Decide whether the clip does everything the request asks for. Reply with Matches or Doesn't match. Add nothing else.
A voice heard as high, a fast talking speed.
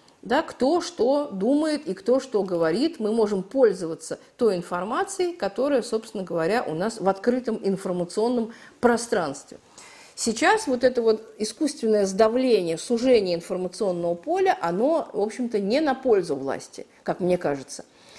Doesn't match